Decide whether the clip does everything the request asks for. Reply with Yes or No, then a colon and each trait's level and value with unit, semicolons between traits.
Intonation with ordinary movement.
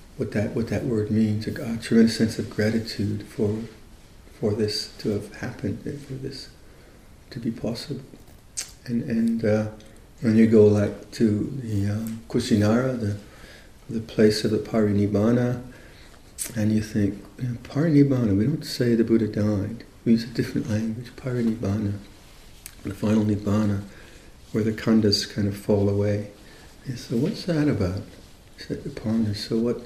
No: narrow, 2.1 semitones